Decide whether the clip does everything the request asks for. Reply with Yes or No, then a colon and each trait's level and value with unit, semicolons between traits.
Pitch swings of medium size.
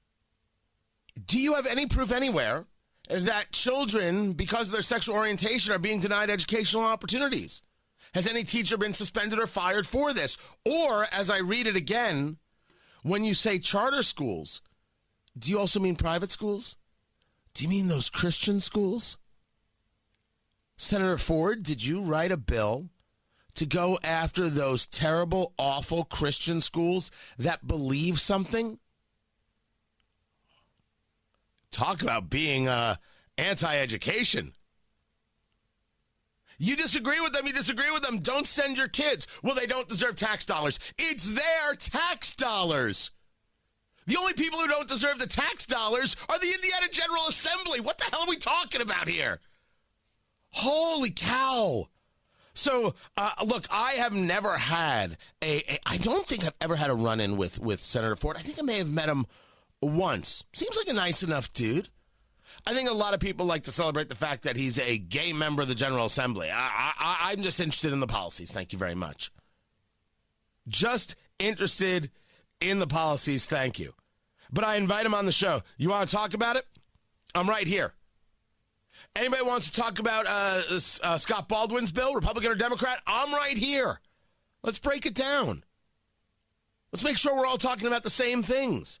No: wide, 8.9 semitones